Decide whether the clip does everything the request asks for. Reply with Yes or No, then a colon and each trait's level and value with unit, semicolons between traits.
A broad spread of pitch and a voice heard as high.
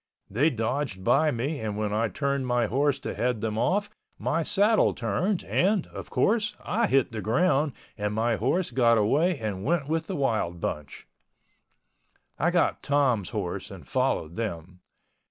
No: wide, 6.8 semitones; low, 125 Hz